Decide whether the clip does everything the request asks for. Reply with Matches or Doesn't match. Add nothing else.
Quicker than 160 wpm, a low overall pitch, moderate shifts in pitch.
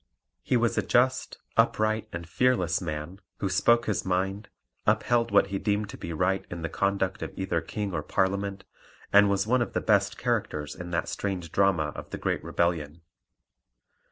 Matches